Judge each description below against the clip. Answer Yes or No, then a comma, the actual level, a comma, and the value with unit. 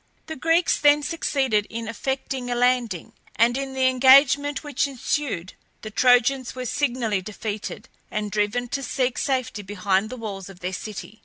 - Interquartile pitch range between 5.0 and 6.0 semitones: No, average, 4.2 semitones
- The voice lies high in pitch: Yes, high, 245 Hz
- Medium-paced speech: Yes, average, 160 wpm